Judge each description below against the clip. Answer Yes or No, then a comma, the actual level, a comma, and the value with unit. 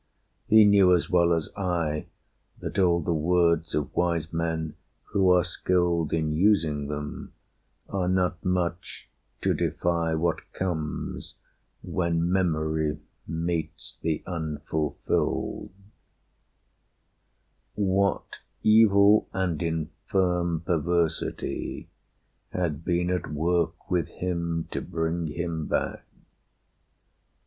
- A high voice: No, very low, 85 Hz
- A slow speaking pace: Yes, slow, 100 wpm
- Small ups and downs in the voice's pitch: Yes, narrow, 2.1 semitones